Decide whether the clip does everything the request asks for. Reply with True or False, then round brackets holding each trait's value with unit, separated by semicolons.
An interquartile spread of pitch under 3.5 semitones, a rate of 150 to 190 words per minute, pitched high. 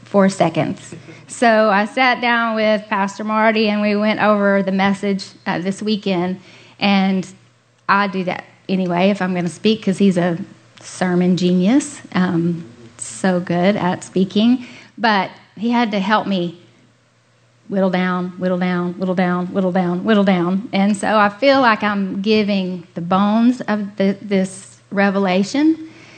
True (2.7 semitones; 155 wpm; 195 Hz)